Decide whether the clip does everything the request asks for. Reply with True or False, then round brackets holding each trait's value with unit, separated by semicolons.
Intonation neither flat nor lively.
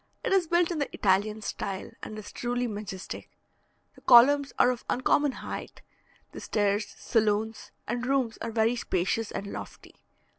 True (3.5 semitones)